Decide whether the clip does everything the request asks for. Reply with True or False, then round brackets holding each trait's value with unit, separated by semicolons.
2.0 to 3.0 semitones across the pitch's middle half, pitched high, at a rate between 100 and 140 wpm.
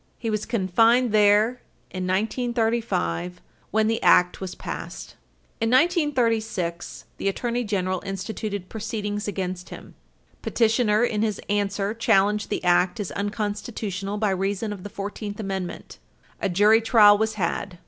True (2.6 semitones; 205 Hz; 135 wpm)